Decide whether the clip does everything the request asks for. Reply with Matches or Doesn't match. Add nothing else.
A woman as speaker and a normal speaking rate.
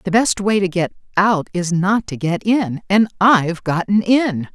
Matches